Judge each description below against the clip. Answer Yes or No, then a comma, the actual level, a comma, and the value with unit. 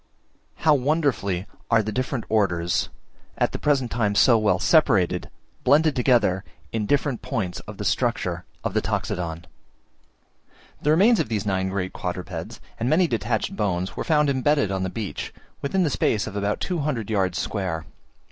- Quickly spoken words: No, average, 160 wpm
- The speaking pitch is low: Yes, low, 110 Hz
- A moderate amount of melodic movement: No, wide, 6.9 semitones